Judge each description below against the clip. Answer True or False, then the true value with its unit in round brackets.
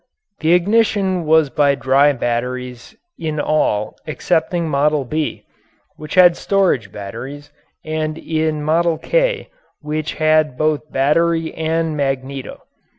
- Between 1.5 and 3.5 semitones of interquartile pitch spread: True (2.9 semitones)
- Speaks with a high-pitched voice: False (155 Hz)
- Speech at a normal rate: False (115 wpm)